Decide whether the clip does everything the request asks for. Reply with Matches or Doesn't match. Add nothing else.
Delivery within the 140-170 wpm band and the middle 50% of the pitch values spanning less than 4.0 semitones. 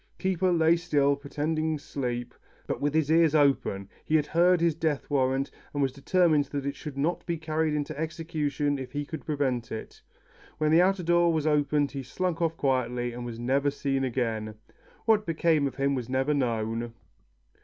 Doesn't match